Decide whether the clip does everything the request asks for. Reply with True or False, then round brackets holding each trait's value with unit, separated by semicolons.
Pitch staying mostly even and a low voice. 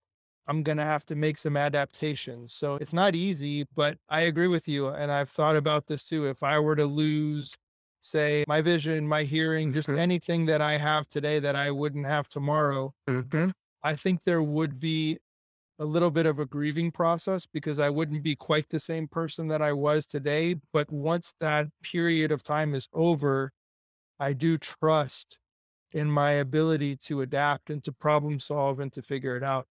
False (1.8 semitones; 150 Hz)